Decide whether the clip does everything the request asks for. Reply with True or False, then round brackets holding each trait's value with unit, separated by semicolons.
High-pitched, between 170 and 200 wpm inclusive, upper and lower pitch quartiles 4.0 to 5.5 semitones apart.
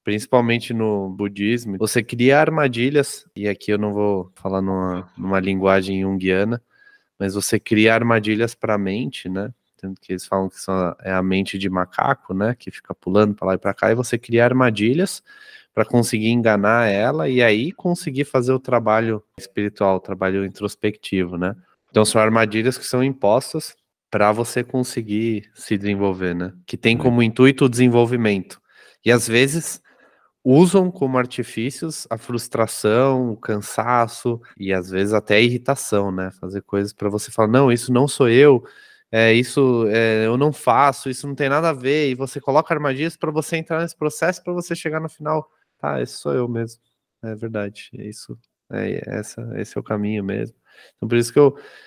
False (115 Hz; 180 wpm; 4.4 semitones)